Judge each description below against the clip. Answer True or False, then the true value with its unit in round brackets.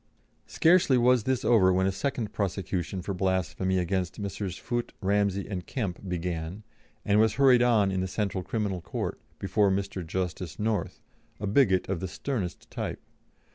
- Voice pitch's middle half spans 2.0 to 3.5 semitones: True (3.0 semitones)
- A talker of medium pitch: False (100 Hz)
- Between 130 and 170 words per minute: True (160 wpm)